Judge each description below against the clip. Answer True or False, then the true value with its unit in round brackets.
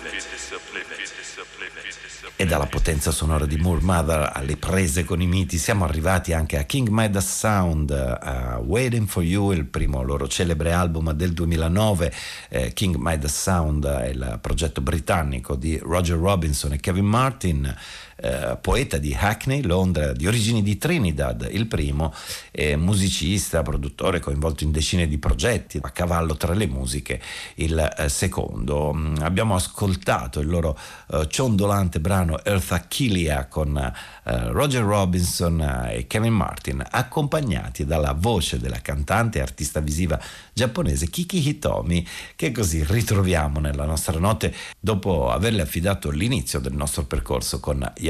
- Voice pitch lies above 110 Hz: False (85 Hz)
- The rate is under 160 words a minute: True (135 wpm)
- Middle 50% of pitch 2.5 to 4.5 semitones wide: False (5.0 semitones)